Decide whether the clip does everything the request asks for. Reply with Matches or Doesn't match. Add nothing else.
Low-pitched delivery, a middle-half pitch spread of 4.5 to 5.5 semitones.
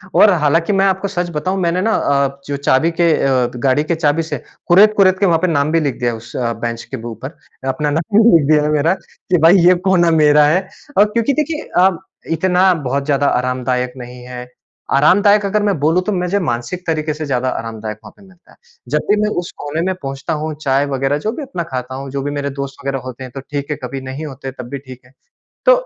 Doesn't match